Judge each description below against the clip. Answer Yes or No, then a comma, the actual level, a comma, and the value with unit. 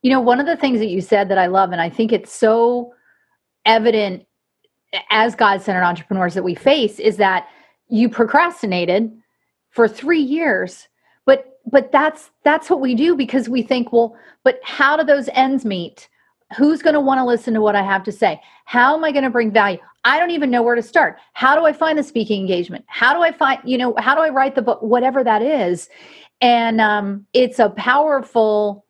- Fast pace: Yes, fast, 210 wpm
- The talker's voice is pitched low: No, high, 240 Hz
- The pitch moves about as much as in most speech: Yes, average, 4.3 semitones